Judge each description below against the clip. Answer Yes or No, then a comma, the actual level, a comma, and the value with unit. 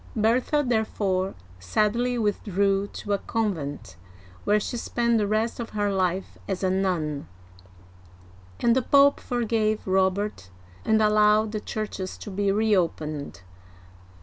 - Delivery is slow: Yes, slow, 125 wpm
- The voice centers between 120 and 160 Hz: No, high, 210 Hz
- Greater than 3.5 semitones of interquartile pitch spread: No, average, 2.8 semitones